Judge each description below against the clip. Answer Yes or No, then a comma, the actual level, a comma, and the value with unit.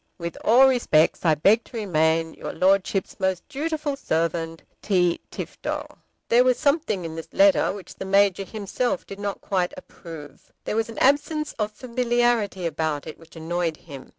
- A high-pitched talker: Yes, high, 195 Hz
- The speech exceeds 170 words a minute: No, average, 165 wpm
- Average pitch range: No, wide, 6.6 semitones